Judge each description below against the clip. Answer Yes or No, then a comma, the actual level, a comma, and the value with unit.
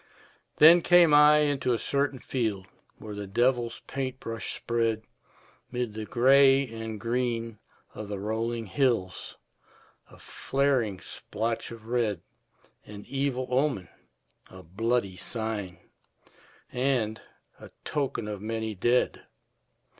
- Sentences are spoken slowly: Yes, slow, 115 wpm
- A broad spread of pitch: No, average, 3.6 semitones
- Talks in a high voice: No, low, 115 Hz